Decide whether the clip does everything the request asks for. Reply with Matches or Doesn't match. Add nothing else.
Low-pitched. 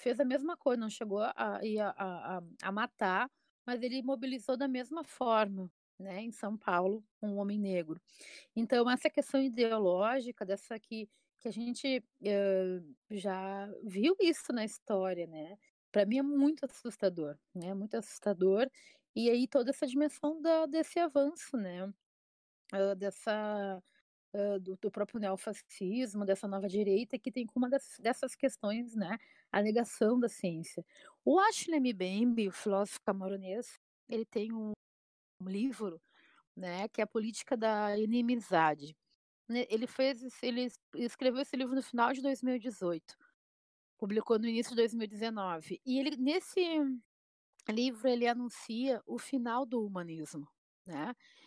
Doesn't match